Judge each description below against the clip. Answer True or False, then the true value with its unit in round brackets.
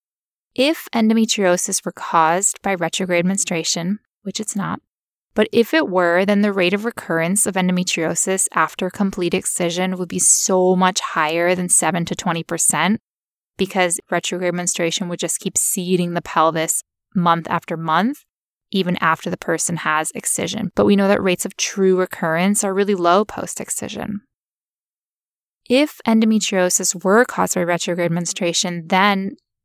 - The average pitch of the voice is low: False (185 Hz)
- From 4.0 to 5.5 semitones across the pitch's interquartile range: False (2.6 semitones)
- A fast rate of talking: False (145 wpm)